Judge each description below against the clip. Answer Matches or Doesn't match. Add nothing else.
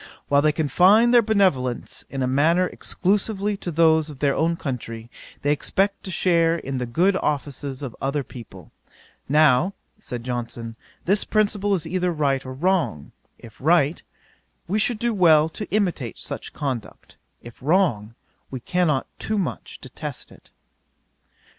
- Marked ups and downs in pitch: Matches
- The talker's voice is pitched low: Doesn't match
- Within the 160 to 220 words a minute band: Doesn't match